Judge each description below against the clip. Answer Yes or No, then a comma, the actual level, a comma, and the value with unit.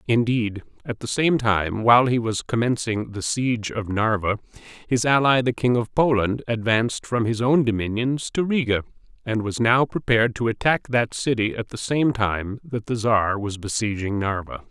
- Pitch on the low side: Yes, low, 115 Hz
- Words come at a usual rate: Yes, average, 180 wpm